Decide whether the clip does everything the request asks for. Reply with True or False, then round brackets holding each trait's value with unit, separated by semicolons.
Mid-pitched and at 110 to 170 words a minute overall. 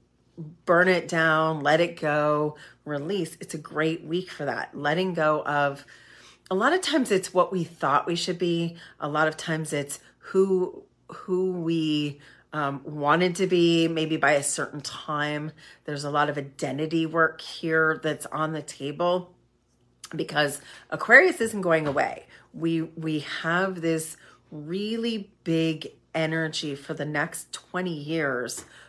True (160 Hz; 150 wpm)